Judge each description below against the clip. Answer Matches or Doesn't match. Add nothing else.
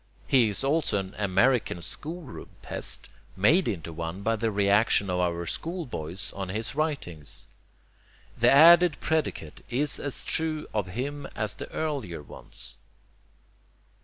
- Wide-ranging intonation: Matches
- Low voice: Matches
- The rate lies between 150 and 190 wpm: Doesn't match